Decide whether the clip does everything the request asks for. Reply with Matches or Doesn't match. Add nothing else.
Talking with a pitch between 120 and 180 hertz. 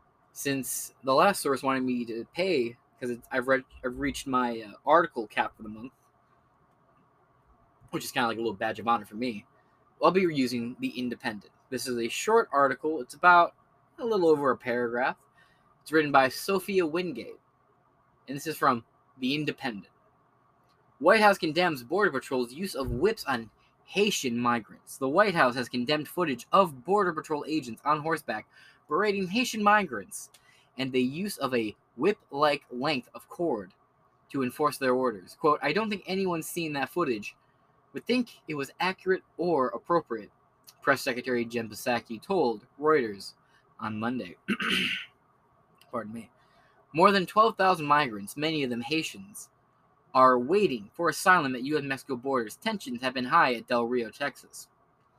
Matches